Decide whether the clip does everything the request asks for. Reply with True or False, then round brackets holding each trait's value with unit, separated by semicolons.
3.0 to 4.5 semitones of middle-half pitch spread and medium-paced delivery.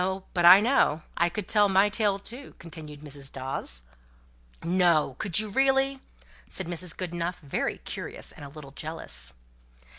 False (5.3 semitones; 150 wpm)